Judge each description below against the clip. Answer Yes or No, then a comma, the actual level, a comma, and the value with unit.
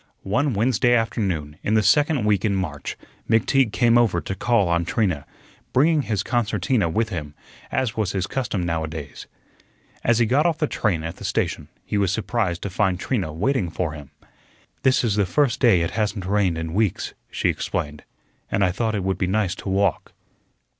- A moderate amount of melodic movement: Yes, average, 5.0 semitones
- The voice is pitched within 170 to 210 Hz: No, low, 100 Hz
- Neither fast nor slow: Yes, average, 190 wpm